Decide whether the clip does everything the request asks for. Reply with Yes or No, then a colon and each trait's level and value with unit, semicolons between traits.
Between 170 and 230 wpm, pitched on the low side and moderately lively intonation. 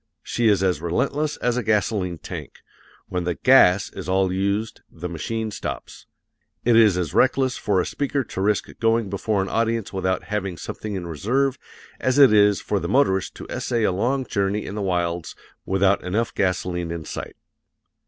Yes: average, 180 wpm; low, 100 Hz; average, 3.8 semitones